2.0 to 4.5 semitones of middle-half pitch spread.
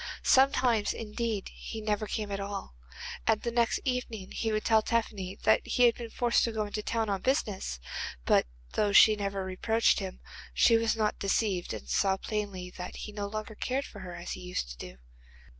Yes: average, 2.7 semitones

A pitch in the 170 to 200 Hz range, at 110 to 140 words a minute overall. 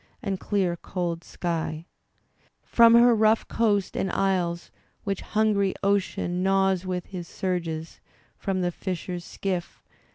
Yes: medium, 185 Hz; slow, 135 wpm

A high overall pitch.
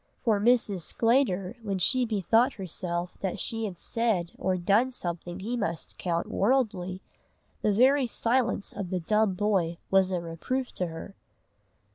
Yes: high, 200 Hz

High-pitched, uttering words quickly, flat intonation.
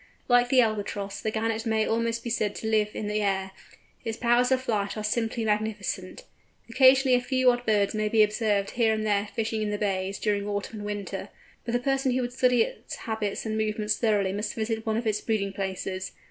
Yes: high, 220 Hz; fast, 215 wpm; narrow, 2.1 semitones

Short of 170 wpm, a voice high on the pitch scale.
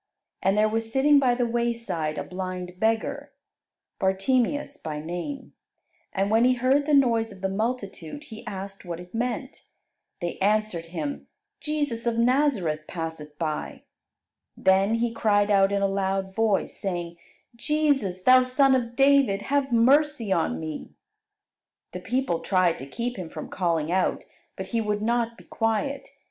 Yes: average, 155 wpm; high, 215 Hz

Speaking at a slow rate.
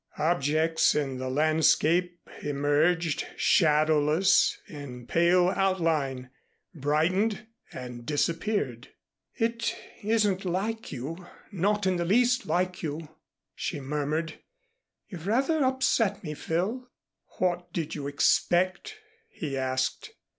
Yes: slow, 105 wpm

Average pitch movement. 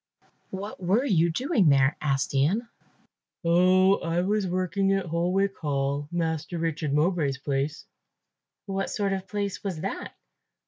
Yes: average, 4.3 semitones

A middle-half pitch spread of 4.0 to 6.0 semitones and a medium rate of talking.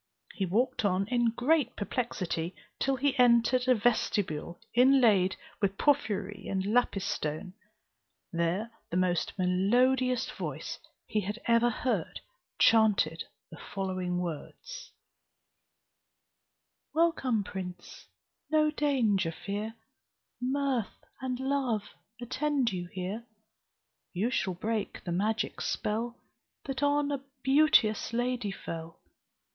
No: average, 5.2 semitones; slow, 110 wpm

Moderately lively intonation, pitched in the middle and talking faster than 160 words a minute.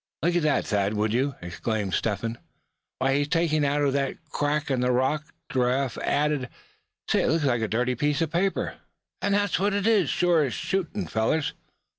Yes: average, 5.0 semitones; medium, 145 Hz; average, 185 wpm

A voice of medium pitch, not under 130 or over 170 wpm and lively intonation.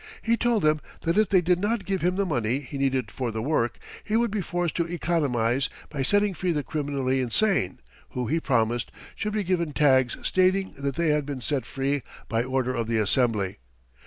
No: medium, 145 Hz; fast, 205 wpm; wide, 6.3 semitones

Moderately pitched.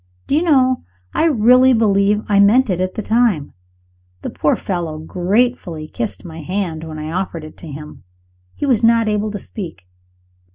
No: high, 200 Hz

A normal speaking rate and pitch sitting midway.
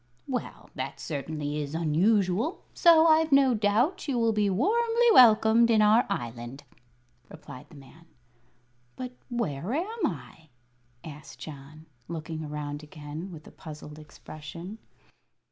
No: slow, 130 wpm; medium, 170 Hz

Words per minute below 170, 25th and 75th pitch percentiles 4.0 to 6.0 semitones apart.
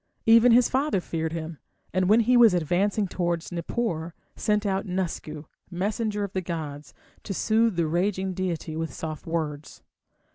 Yes: average, 155 wpm; average, 4.4 semitones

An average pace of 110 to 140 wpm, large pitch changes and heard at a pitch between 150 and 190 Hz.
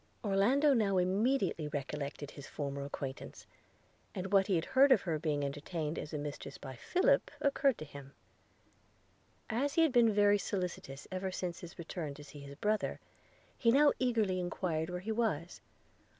No: average, 165 wpm; wide, 6.8 semitones; medium, 185 Hz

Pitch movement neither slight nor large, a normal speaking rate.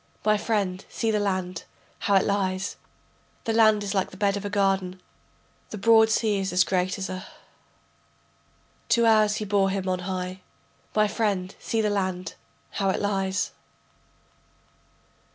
No: narrow, 2.1 semitones; average, 160 wpm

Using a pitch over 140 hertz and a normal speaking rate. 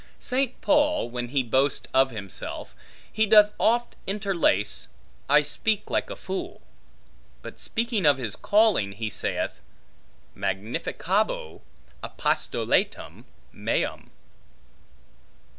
No: medium, 185 Hz; slow, 100 wpm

